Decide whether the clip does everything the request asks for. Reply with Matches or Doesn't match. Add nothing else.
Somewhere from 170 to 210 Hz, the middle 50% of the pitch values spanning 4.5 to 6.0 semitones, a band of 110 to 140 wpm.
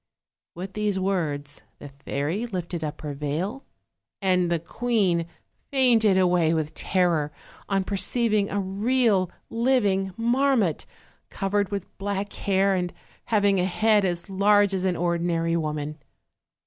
Doesn't match